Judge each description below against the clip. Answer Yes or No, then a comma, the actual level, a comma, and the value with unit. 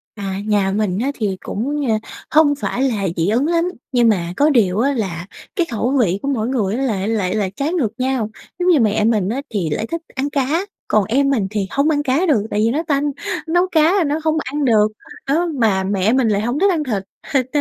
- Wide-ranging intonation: Yes, wide, 5.8 semitones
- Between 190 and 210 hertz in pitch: No, high, 240 Hz